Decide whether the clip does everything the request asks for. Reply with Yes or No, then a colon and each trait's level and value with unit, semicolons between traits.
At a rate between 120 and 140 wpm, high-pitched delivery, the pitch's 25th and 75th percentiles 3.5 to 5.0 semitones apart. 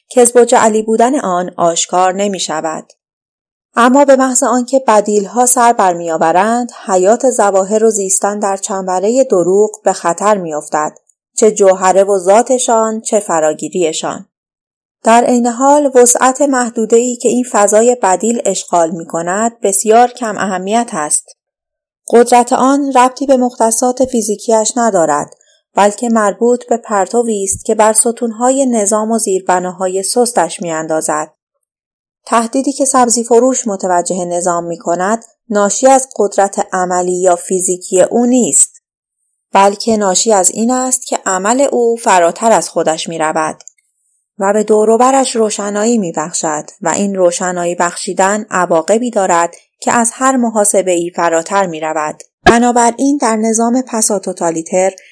Yes: average, 135 wpm; high, 215 Hz; average, 4.6 semitones